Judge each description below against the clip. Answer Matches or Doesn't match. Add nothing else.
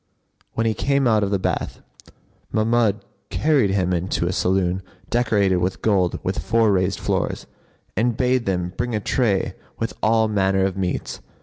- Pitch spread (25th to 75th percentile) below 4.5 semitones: Matches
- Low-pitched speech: Matches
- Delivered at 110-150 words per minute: Doesn't match